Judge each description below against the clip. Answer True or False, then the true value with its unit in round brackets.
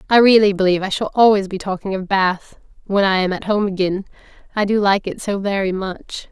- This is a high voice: True (195 Hz)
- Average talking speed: False (210 wpm)